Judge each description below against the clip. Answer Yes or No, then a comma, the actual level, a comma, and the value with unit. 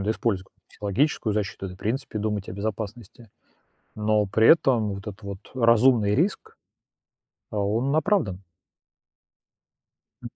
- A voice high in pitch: No, low, 110 Hz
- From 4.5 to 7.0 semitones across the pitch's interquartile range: No, average, 2.9 semitones